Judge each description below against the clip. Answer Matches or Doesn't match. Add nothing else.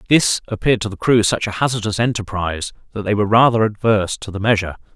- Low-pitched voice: Matches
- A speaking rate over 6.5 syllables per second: Matches